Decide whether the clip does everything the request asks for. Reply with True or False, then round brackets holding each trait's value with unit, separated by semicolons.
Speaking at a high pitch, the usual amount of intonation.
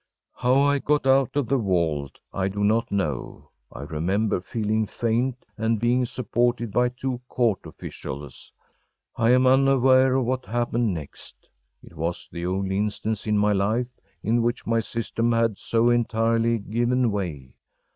False (115 Hz; 3.8 semitones)